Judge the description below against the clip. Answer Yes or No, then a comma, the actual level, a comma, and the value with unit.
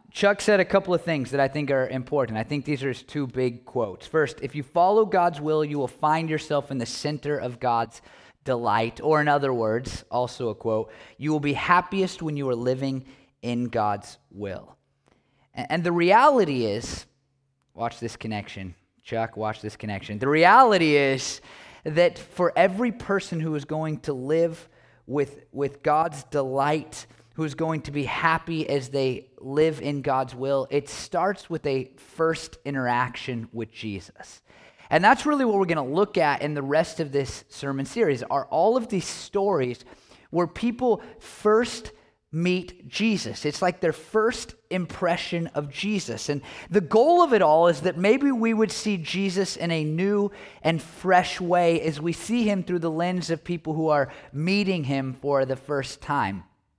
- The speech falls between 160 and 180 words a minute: Yes, average, 175 wpm